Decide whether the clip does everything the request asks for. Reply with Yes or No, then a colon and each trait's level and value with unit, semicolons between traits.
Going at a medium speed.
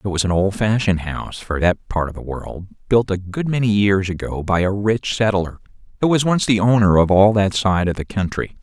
No: fast, 230 wpm